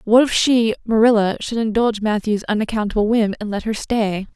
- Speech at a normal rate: Yes, average, 180 wpm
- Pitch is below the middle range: No, high, 220 Hz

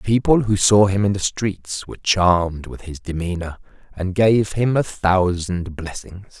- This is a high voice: No, very low, 95 Hz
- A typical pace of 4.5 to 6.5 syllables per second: No, 4.3 syllables/s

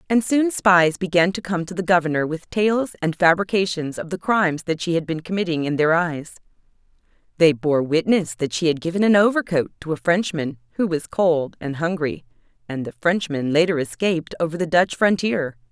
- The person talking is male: No, female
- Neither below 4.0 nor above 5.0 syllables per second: No, 5.3 syllables/s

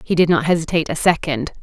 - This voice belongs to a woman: Yes, female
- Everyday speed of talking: No, fast, 220 wpm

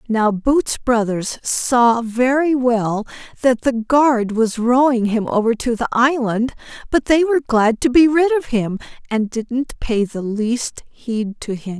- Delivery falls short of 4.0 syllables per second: Yes, 3.7 syllables/s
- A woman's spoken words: Yes, female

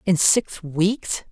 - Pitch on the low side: No, medium, 185 Hz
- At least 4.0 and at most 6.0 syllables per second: No, 2.6 syllables/s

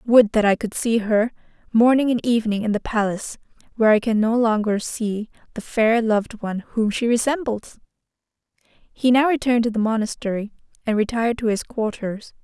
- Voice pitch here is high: Yes, high, 225 Hz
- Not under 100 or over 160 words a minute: No, average, 175 wpm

